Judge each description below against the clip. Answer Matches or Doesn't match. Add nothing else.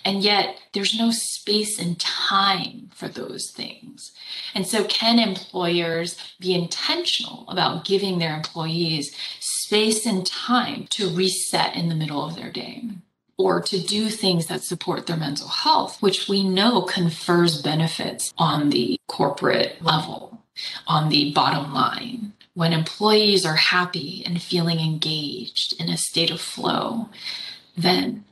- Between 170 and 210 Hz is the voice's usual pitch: Matches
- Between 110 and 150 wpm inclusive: Matches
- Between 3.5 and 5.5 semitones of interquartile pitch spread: Matches